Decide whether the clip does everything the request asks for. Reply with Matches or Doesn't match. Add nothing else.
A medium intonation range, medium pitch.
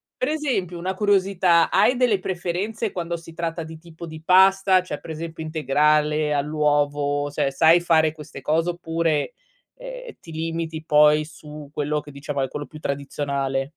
Matches